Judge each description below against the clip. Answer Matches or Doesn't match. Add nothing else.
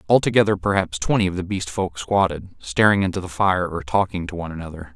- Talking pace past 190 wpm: Matches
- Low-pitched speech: Matches